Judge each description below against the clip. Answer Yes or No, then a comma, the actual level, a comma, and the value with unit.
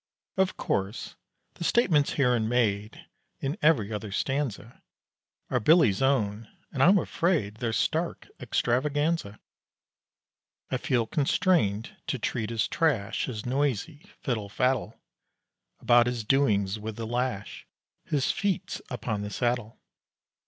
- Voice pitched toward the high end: No, low, 120 Hz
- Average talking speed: No, slow, 120 wpm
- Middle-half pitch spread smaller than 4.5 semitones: No, average, 5.2 semitones